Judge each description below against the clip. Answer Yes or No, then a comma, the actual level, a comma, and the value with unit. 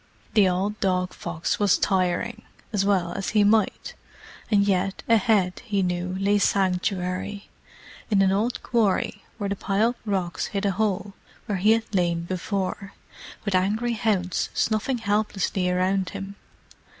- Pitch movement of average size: No, narrow, 2.3 semitones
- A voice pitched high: Yes, high, 195 Hz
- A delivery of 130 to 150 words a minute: Yes, average, 140 wpm